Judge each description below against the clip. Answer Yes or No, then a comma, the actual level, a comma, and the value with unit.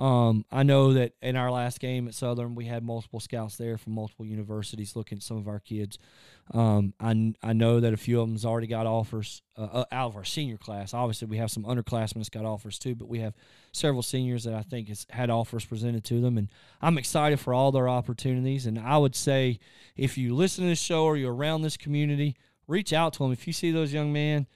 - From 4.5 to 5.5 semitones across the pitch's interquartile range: No, average, 3.3 semitones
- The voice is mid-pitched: No, low, 120 Hz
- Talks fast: Yes, fast, 235 wpm